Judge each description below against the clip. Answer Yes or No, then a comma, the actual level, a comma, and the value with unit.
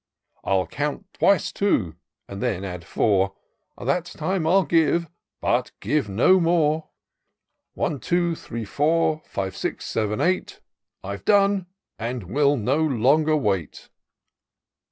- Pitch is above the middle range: No, medium, 145 Hz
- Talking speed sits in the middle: No, slow, 125 wpm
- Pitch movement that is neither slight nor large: No, wide, 8.4 semitones